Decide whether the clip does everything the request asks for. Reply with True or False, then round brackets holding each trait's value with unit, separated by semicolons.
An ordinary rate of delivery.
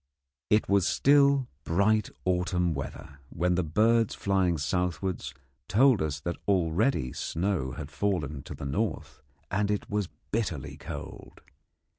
False (130 wpm)